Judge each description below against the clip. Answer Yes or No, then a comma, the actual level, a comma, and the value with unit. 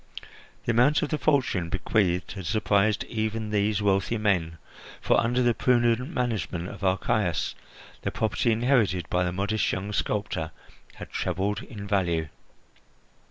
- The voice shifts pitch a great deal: No, average, 3.9 semitones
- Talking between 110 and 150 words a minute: Yes, average, 140 wpm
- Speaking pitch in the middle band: No, low, 105 Hz